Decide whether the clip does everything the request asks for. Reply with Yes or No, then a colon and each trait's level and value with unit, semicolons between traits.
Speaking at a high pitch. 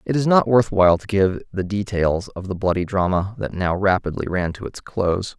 No: very low, 95 Hz